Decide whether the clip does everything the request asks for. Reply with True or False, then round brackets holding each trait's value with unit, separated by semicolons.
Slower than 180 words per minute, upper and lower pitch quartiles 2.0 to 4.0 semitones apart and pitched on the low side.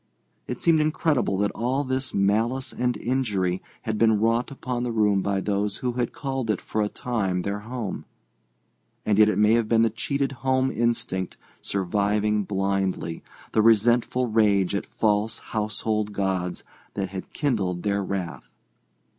True (155 wpm; 3.5 semitones; 110 Hz)